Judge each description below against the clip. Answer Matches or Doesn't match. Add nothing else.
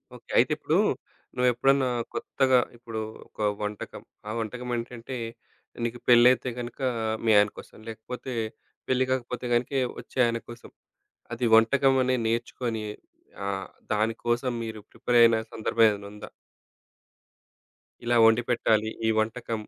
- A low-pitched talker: Matches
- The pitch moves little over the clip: Matches